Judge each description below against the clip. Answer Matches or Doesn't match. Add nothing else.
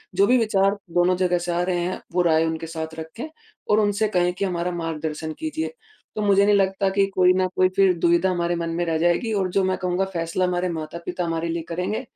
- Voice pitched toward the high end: Doesn't match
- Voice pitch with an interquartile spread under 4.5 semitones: Matches